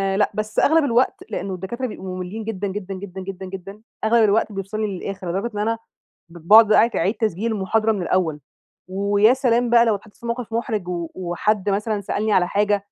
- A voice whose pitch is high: Yes, high, 205 Hz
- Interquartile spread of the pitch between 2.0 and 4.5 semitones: Yes, average, 2.8 semitones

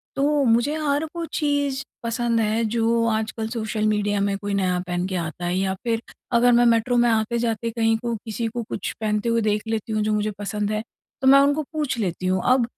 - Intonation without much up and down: Yes, narrow, 2.3 semitones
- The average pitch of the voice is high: Yes, high, 225 Hz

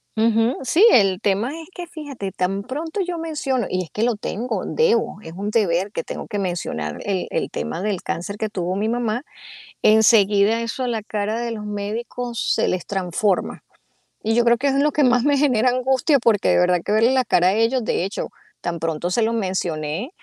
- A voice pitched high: Yes, high, 220 Hz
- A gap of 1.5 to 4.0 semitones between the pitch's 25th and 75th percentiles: No, average, 4.5 semitones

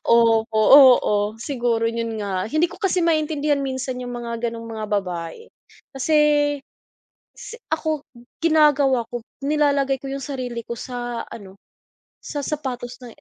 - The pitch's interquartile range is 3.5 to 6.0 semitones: Yes, average, 4.1 semitones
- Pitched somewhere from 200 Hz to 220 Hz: No, very high, 250 Hz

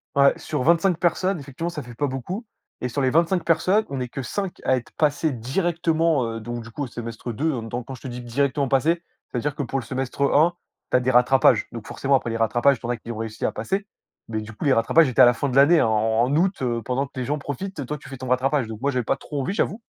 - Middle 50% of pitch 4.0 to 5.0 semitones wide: Yes, average, 4.4 semitones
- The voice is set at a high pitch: No, low, 135 Hz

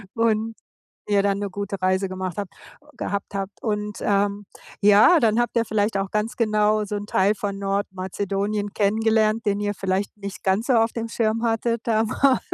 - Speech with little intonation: Yes, narrow, 1.9 semitones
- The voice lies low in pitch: No, high, 205 Hz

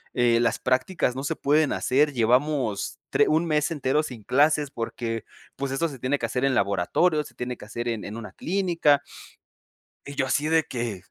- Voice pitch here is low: Yes, low, 130 Hz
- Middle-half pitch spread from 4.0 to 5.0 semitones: Yes, average, 4.3 semitones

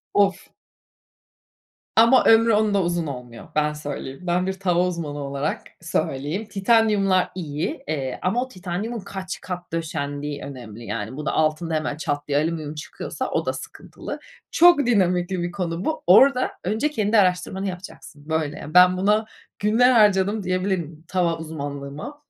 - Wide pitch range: No, average, 4.9 semitones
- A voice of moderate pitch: Yes, medium, 175 Hz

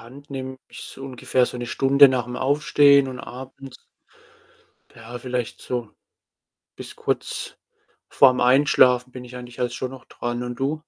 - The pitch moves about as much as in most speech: No, narrow, 1.6 semitones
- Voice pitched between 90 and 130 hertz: Yes, low, 125 Hz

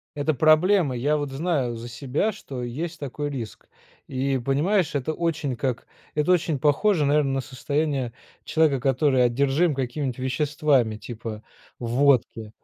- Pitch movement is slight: No, average, 3.2 semitones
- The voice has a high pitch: No, medium, 140 Hz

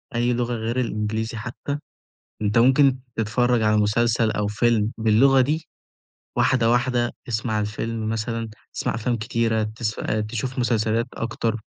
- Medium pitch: No, low, 115 Hz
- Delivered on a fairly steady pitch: Yes, narrow, 2.0 semitones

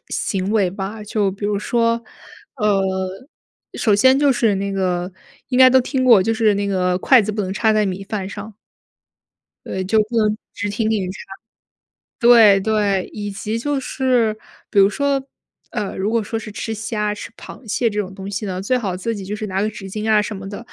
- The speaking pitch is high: Yes, high, 210 Hz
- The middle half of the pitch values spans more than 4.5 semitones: No, narrow, 2.5 semitones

